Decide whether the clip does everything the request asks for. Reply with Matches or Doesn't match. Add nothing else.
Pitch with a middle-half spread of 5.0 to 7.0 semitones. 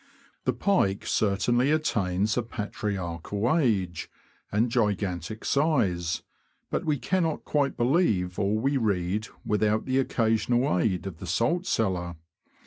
Matches